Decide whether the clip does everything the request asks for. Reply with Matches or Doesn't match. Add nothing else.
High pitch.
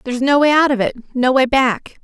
Matches